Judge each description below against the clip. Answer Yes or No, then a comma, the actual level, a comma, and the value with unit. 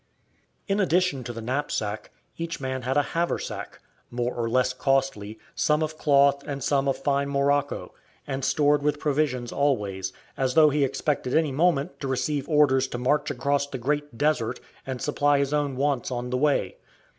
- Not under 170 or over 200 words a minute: Yes, average, 175 wpm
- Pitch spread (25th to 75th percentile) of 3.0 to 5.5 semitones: No, narrow, 2.4 semitones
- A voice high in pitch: No, medium, 140 Hz